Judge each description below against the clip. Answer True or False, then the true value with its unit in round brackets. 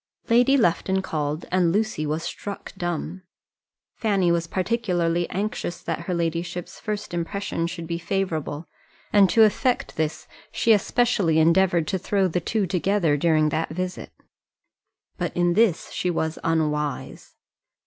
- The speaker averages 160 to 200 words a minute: False (140 wpm)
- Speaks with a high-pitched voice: False (175 Hz)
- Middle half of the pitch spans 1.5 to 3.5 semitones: True (3.2 semitones)